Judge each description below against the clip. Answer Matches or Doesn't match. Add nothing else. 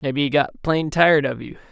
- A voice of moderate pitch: Matches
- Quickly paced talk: Matches